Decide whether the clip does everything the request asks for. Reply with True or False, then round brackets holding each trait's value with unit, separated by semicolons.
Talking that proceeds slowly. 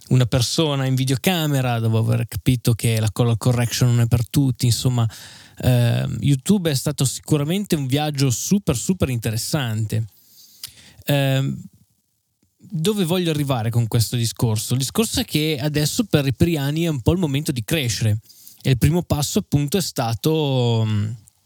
False (155 wpm)